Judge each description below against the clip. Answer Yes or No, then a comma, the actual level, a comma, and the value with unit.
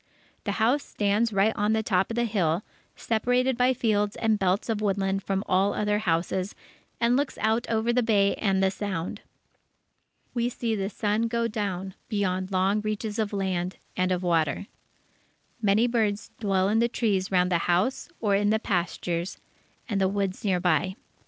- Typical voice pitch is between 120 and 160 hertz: No, high, 205 Hz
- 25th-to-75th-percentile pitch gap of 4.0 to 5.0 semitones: No, average, 2.9 semitones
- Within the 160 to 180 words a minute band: Yes, average, 175 wpm